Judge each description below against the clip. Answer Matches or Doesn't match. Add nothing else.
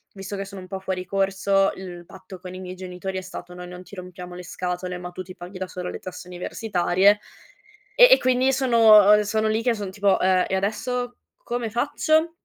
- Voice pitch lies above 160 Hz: Matches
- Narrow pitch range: Doesn't match